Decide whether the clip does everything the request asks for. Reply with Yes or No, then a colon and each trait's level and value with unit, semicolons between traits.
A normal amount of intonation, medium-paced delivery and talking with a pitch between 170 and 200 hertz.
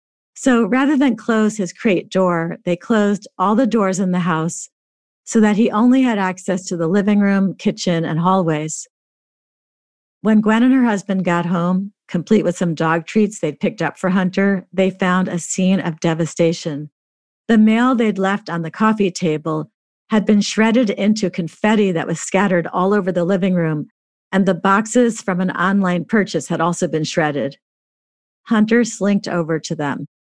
Yes: average, 3.9 semitones; average, 175 wpm; high, 190 Hz